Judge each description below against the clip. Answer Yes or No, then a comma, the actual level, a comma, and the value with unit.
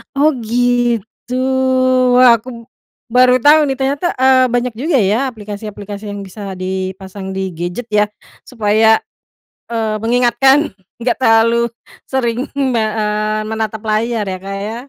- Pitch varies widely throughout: No, average, 2.9 semitones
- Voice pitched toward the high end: Yes, high, 225 Hz